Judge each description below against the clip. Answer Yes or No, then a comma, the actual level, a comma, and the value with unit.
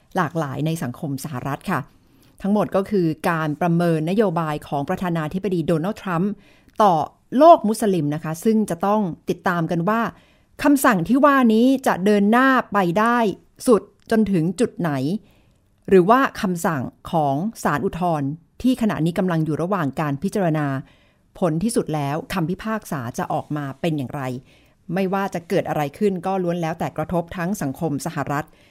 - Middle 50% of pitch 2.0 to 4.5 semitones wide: No, average, 5.3 semitones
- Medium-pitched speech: Yes, medium, 175 Hz